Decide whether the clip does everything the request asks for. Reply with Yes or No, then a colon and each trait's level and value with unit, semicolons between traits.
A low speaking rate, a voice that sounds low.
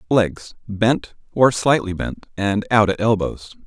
Yes: slow, 130 wpm; low, 105 Hz